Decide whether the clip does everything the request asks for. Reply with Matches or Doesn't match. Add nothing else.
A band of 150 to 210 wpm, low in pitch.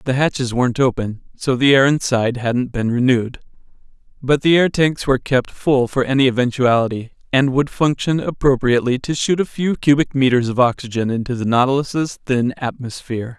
Matches